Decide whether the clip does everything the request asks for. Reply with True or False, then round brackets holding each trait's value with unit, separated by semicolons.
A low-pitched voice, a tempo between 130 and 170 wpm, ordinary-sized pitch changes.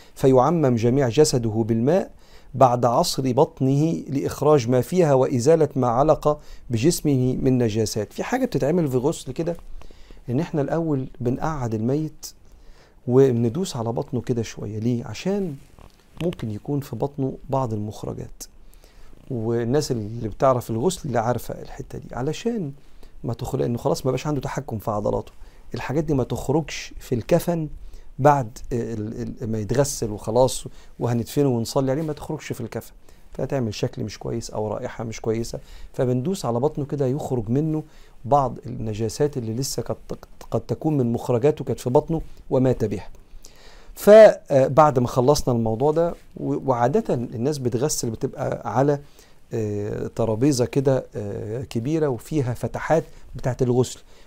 True (130 Hz; 135 wpm; 4.0 semitones)